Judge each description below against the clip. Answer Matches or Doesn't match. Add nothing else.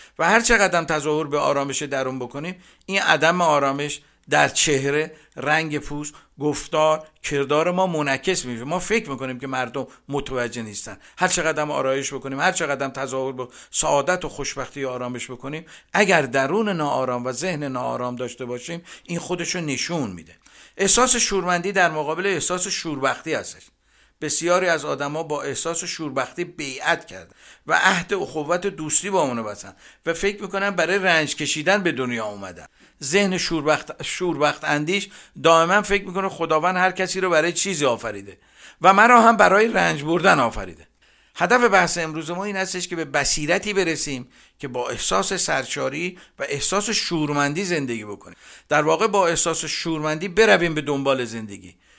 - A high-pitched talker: Doesn't match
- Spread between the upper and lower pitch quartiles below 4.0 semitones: Doesn't match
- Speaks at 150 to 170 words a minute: Matches